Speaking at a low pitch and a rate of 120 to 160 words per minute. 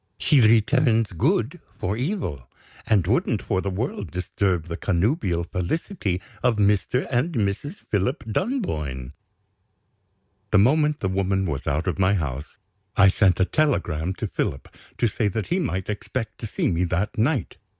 Yes: low, 100 Hz; average, 155 wpm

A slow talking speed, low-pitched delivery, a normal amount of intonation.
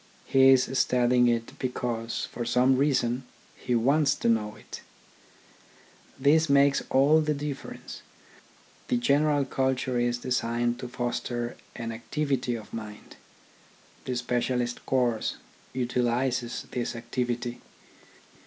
No: slow, 115 wpm; low, 125 Hz; narrow, 1.8 semitones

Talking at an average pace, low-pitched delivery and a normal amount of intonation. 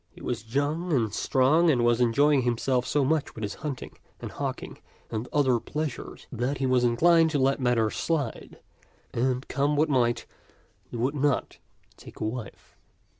Yes: average, 175 wpm; low, 130 Hz; average, 3.5 semitones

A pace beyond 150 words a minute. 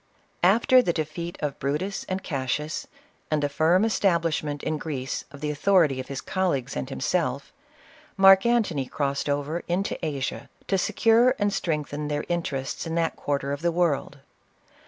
Yes: average, 160 wpm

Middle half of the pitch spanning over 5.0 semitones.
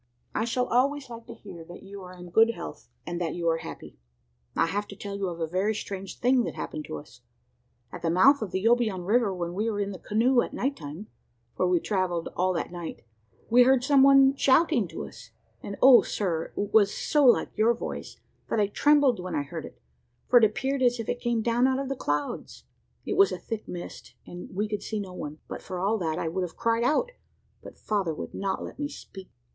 Yes: wide, 5.4 semitones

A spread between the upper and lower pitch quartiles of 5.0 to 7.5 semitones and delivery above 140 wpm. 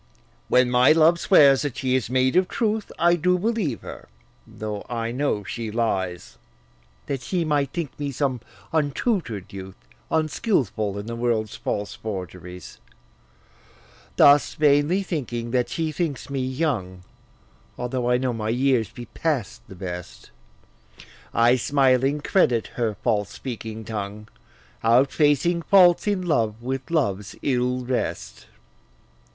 No: average, 5.3 semitones; slow, 135 wpm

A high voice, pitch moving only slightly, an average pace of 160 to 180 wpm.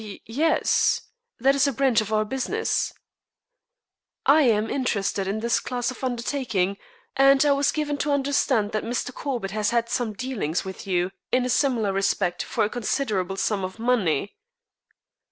No: high, 235 Hz; average, 4.7 semitones; average, 165 wpm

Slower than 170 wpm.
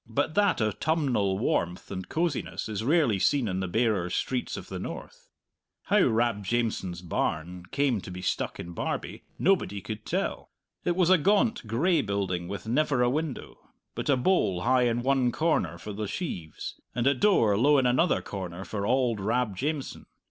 No: average, 175 wpm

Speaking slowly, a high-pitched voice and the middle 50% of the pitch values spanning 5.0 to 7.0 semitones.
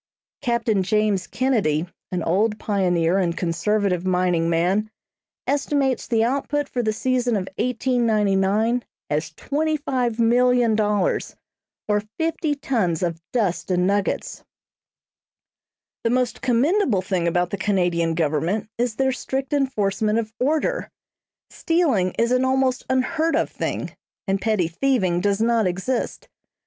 Yes: slow, 120 wpm; high, 215 Hz; wide, 5.6 semitones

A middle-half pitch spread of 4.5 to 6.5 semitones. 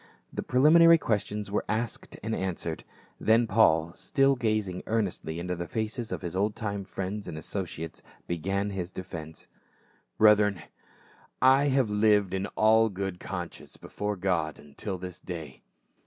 No: average, 3.7 semitones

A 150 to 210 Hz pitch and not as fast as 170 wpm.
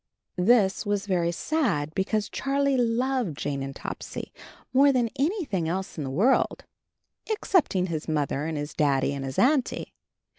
Yes: high, 190 Hz; average, 150 wpm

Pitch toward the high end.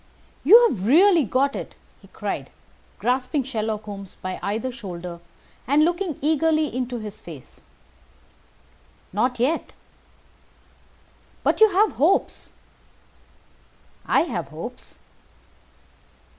Yes: very high, 255 Hz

